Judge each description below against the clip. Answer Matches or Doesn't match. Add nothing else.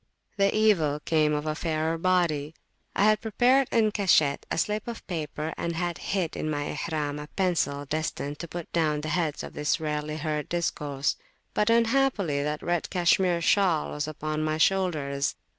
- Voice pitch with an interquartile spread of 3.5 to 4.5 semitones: Matches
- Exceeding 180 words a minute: Doesn't match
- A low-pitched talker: Doesn't match